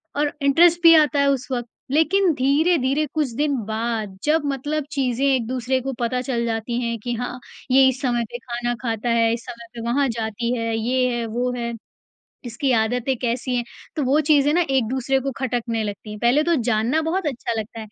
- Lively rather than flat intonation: No, average, 3.1 semitones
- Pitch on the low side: No, very high, 250 Hz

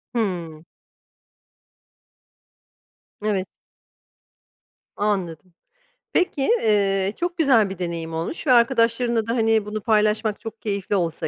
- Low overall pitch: No, high, 210 Hz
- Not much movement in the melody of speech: No, average, 3.4 semitones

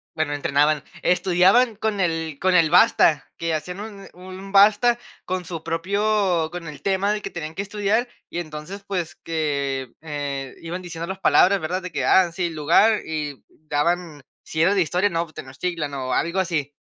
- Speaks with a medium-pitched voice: Yes, medium, 170 Hz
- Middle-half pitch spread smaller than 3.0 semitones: No, average, 3.9 semitones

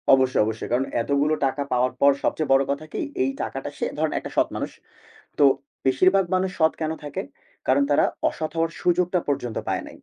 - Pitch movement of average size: Yes, average, 3.3 semitones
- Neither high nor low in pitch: Yes, medium, 145 Hz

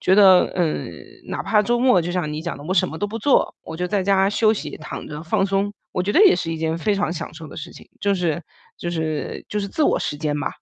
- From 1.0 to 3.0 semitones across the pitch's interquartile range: No, average, 4.1 semitones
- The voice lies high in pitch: No, medium, 180 Hz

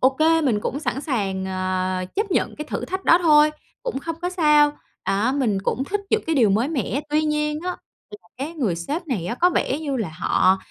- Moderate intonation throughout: No, wide, 7.3 semitones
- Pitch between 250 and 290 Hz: Yes, very high, 280 Hz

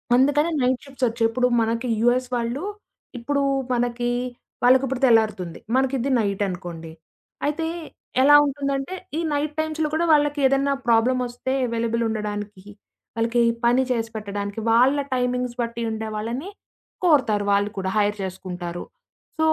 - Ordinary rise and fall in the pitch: Yes, average, 4.0 semitones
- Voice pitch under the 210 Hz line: No, high, 240 Hz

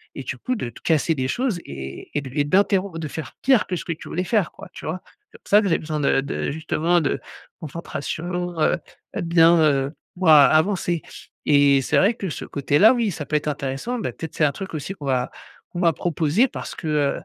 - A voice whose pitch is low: No, medium, 160 Hz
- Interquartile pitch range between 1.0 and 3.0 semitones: No, average, 4.3 semitones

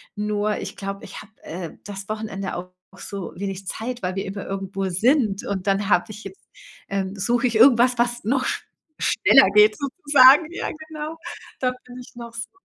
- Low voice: No, high, 215 Hz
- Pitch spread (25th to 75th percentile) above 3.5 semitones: Yes, average, 4.3 semitones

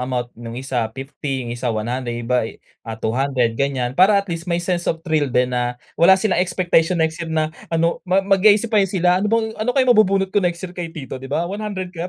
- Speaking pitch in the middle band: Yes, medium, 165 Hz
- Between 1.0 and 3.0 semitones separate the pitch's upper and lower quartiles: No, wide, 6.5 semitones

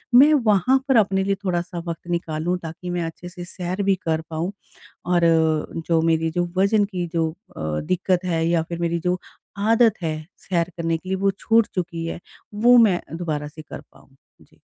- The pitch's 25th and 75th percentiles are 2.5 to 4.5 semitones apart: Yes, average, 3.0 semitones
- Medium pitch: Yes, medium, 175 Hz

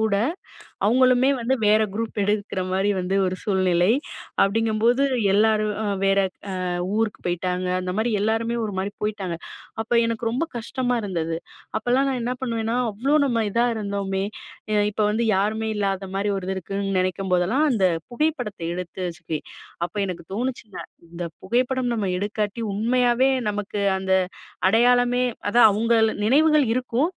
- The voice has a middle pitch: No, high, 215 Hz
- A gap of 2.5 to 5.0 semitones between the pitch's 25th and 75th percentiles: Yes, average, 3.7 semitones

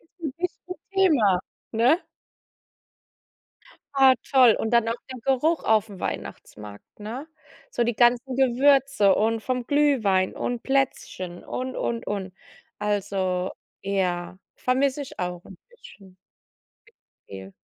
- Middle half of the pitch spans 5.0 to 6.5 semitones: Yes, wide, 5.6 semitones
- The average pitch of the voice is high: Yes, high, 235 Hz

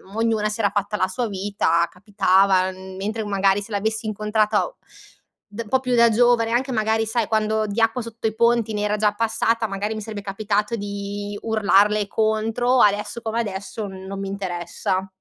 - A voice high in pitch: Yes, high, 210 Hz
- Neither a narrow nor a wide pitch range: No, narrow, 2.1 semitones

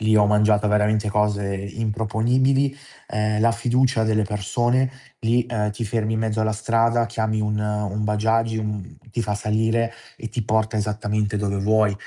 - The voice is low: Yes, low, 110 Hz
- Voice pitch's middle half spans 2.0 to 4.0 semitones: No, narrow, 1.5 semitones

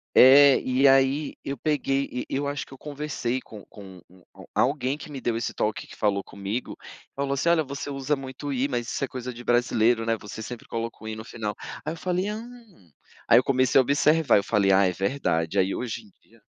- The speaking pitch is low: Yes, low, 130 Hz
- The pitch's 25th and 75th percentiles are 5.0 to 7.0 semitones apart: No, average, 4.1 semitones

